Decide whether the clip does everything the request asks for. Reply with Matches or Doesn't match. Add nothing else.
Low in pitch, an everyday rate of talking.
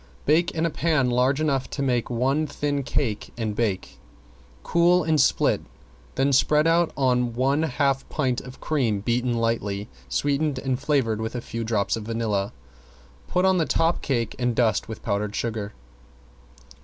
Matches